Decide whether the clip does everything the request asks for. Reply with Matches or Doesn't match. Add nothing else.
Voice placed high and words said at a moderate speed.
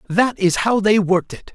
Doesn't match